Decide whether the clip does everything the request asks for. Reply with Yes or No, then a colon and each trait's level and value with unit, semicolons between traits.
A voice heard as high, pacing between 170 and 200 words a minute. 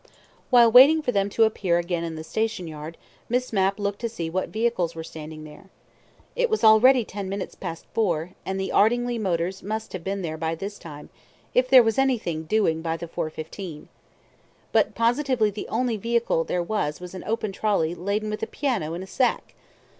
Yes: high, 200 Hz; average, 190 wpm